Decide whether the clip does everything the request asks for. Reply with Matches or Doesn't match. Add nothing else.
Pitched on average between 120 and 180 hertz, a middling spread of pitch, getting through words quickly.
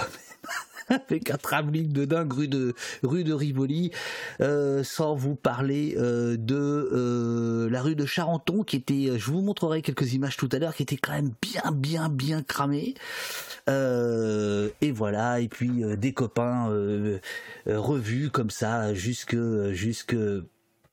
Doesn't match